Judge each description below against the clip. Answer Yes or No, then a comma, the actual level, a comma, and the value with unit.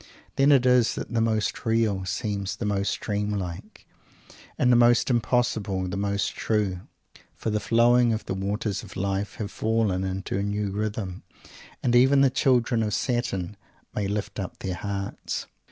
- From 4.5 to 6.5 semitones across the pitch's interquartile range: No, average, 3.2 semitones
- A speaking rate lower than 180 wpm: Yes, average, 170 wpm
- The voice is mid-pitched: No, low, 105 Hz